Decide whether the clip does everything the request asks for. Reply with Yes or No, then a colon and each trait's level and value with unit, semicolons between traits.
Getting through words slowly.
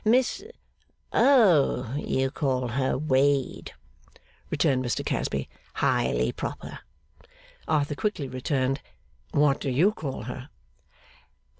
Yes: slow, 100 wpm